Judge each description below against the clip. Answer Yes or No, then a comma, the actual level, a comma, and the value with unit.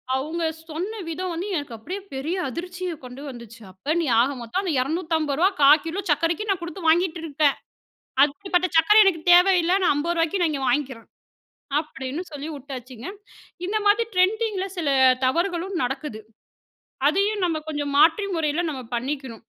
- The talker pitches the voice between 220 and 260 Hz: No, very high, 325 Hz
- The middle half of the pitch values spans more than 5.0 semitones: No, average, 4.7 semitones